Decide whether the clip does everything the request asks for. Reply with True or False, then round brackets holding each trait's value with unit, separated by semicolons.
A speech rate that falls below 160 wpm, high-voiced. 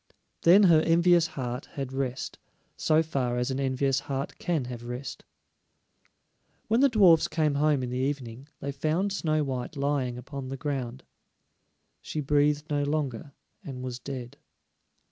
False (150 wpm; 140 Hz)